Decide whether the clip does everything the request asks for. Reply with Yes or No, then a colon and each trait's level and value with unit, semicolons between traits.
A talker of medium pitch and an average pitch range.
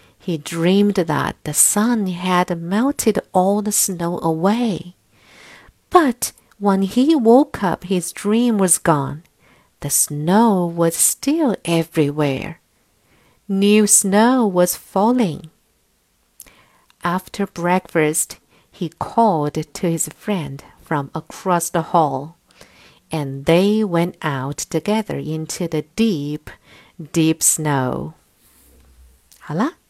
Yes: medium, 175 Hz; average, 4.9 semitones